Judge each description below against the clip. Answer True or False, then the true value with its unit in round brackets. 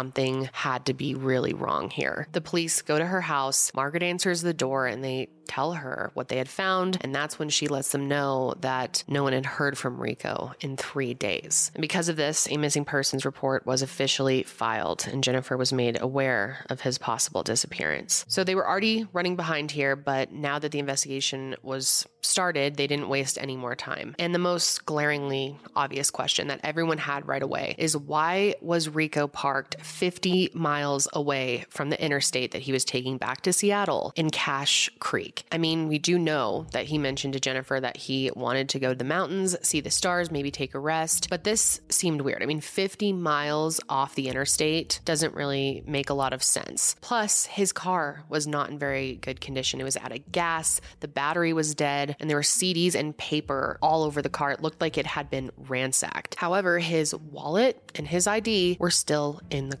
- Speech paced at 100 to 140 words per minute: False (205 wpm)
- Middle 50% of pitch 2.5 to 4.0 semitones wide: True (3.6 semitones)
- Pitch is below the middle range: False (145 Hz)